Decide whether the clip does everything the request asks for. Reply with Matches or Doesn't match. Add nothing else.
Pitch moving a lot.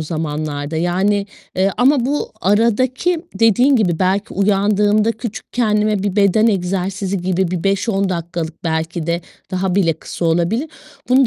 Doesn't match